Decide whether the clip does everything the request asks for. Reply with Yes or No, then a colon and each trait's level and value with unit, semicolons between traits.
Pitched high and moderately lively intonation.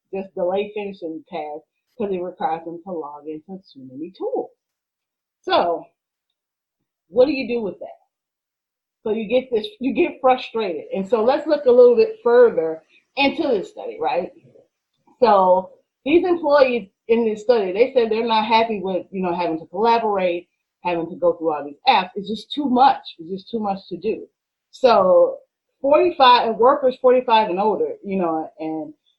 No: high, 225 Hz; wide, 7.7 semitones